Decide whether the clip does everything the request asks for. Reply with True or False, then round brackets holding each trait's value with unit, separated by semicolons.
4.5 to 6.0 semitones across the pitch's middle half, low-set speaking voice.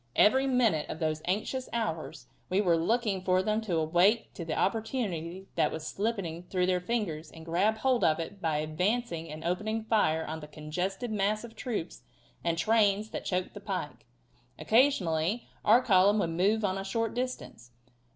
False (5.0 semitones; 190 Hz)